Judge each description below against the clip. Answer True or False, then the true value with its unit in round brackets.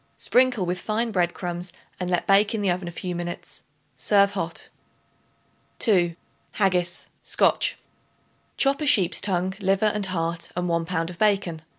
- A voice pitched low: False (185 Hz)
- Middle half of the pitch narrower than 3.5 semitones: True (2.8 semitones)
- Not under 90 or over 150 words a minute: False (160 wpm)